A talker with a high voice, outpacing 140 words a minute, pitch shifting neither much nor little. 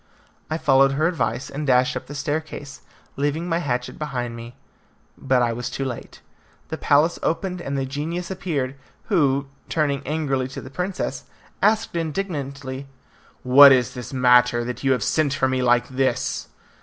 No: medium, 140 Hz; average, 165 wpm; average, 3.5 semitones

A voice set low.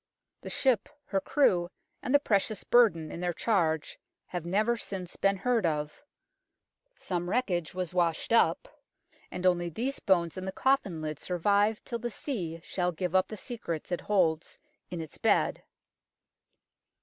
No: medium, 185 Hz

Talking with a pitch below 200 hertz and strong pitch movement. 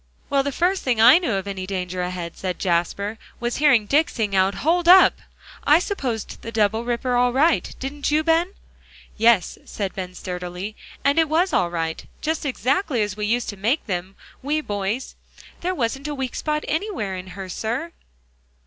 No: high, 235 Hz; wide, 7.5 semitones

